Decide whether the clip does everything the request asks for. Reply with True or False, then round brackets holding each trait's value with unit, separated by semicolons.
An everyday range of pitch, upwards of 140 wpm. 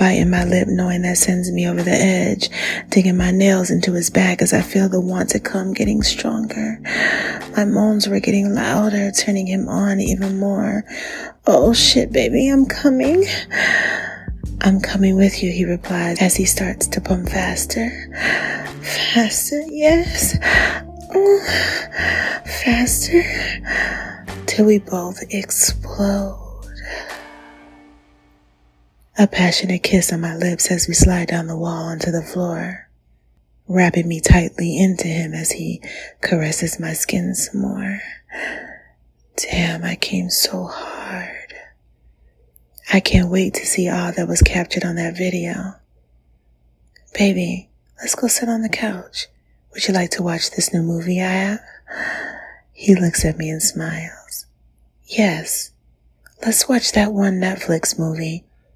False (3.3 semitones; 135 wpm)